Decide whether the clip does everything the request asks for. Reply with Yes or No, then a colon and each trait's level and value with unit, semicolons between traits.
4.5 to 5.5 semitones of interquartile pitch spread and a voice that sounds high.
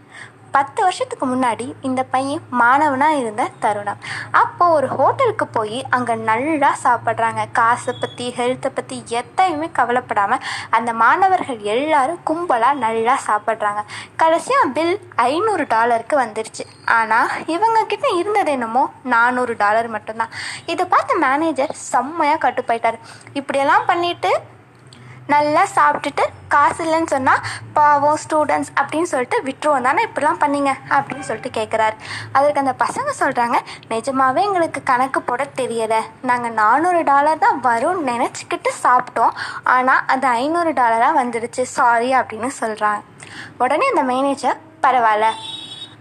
Yes: average, 5.0 semitones; very high, 265 Hz